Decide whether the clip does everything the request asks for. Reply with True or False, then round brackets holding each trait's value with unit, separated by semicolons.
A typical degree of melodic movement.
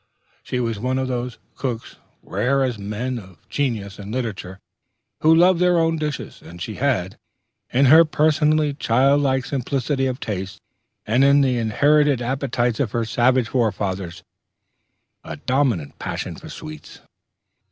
True (4.3 semitones)